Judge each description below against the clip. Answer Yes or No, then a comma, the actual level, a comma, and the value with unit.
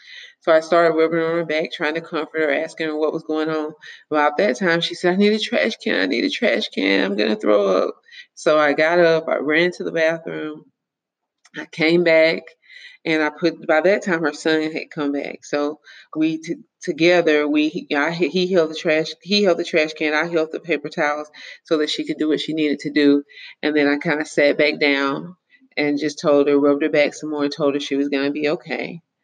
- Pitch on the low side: No, medium, 155 Hz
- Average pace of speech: No, fast, 235 wpm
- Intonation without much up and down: Yes, narrow, 2.3 semitones